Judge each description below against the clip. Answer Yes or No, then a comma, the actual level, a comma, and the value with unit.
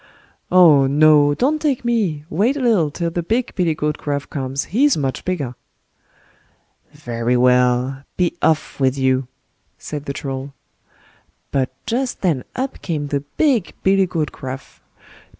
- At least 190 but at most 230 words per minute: No, average, 145 wpm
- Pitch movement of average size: No, wide, 6.2 semitones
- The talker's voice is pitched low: No, medium, 150 Hz